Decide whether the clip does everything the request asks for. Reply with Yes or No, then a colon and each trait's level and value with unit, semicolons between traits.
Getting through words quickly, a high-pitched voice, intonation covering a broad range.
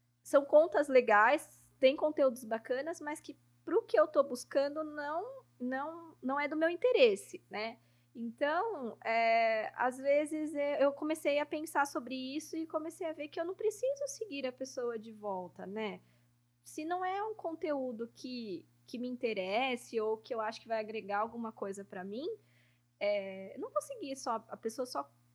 No: average, 175 wpm; very high, 260 Hz; wide, 6.0 semitones